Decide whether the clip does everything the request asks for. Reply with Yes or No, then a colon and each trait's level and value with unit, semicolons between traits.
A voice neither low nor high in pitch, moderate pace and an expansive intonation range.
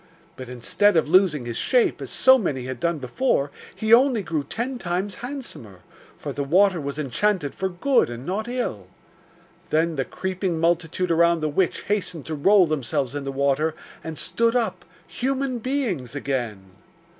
Yes: medium, 170 Hz; average, 165 wpm; wide, 7.0 semitones